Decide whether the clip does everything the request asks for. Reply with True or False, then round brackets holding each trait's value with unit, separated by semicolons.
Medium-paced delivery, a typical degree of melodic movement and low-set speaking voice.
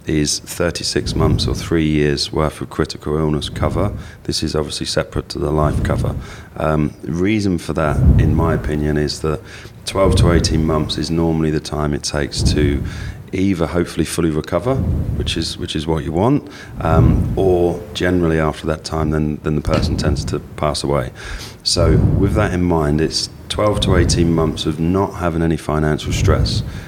True (180 wpm; 3.4 semitones; 80 Hz)